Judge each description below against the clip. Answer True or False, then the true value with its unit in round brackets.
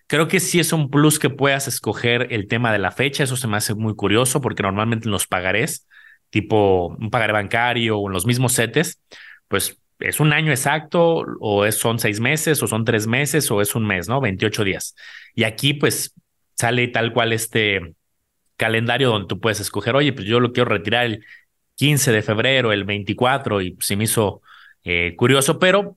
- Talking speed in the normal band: False (195 wpm)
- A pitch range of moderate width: True (4.6 semitones)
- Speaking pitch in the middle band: False (115 Hz)